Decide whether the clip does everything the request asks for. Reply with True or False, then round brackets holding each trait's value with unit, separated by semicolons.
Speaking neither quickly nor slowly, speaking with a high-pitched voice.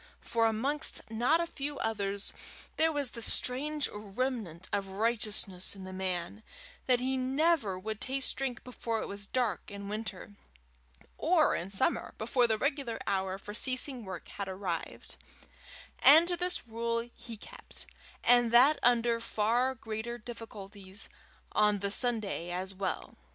True (145 wpm; 225 Hz)